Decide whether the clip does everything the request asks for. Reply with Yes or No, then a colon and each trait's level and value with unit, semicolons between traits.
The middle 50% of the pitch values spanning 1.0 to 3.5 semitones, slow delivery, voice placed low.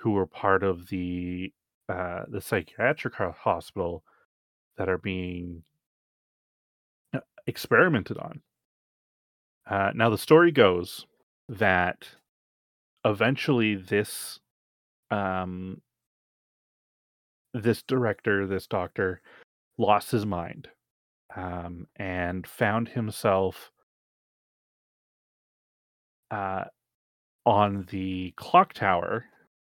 Yes: average, 3.2 semitones; slow, 80 wpm; very low, 95 Hz